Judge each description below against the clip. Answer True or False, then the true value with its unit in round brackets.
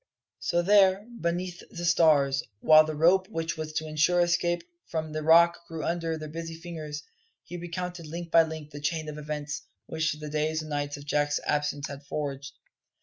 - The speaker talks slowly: False (185 wpm)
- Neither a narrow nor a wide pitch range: False (2.2 semitones)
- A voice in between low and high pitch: True (160 Hz)